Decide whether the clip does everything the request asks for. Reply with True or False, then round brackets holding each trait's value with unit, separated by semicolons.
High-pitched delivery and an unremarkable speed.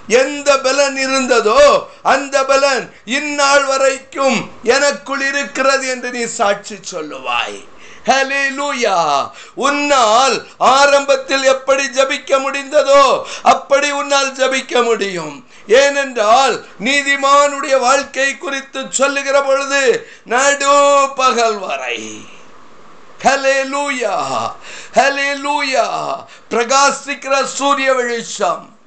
False (275 Hz; 60 wpm)